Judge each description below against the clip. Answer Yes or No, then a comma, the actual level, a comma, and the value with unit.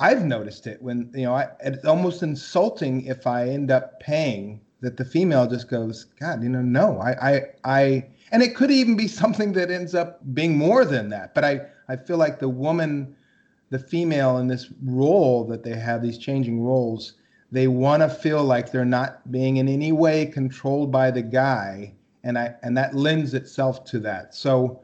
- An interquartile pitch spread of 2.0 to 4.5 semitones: Yes, average, 3.3 semitones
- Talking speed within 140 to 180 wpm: No, average, 200 wpm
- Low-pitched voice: Yes, low, 130 Hz